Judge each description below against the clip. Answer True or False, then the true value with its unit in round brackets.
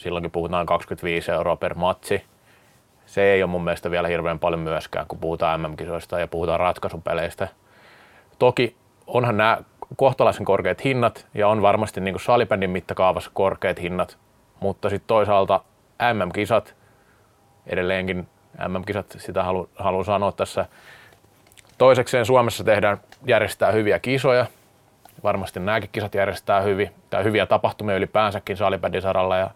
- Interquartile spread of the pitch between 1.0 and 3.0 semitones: False (3.6 semitones)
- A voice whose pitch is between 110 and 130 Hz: False (100 Hz)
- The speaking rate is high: False (130 wpm)